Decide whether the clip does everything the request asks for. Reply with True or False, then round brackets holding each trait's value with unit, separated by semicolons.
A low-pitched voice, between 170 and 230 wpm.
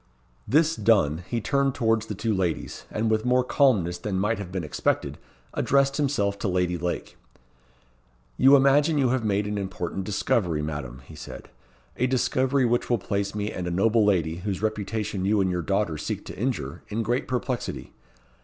True (105 Hz; 180 wpm)